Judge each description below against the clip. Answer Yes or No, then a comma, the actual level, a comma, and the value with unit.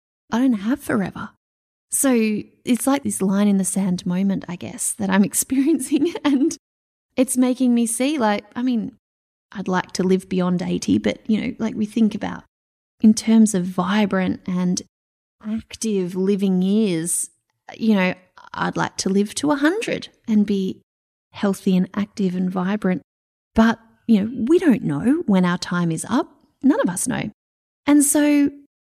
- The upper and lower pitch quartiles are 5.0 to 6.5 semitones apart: Yes, average, 5.3 semitones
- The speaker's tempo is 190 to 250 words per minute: No, average, 165 wpm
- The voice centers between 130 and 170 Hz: No, high, 215 Hz